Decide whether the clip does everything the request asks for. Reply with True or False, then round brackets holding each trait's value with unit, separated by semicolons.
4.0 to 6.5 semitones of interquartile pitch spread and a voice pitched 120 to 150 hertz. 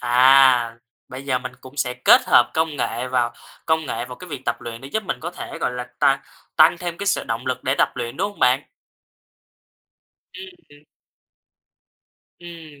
True (4.3 semitones; 135 Hz)